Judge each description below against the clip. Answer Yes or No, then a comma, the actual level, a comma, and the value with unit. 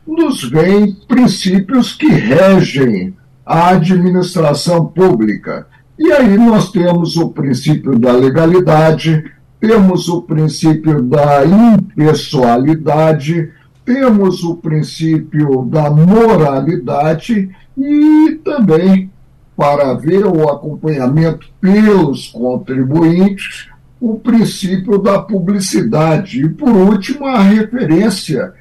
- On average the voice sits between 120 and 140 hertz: No, medium, 175 Hz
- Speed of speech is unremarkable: No, slow, 90 wpm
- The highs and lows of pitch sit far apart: No, average, 4.8 semitones